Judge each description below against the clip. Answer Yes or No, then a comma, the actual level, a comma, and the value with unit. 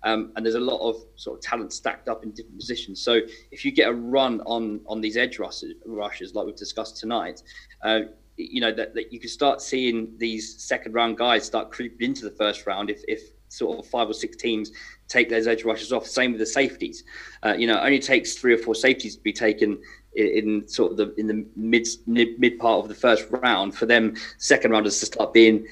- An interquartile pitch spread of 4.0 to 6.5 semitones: No, average, 3.0 semitones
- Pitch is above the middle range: No, low, 115 Hz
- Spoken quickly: Yes, fast, 235 wpm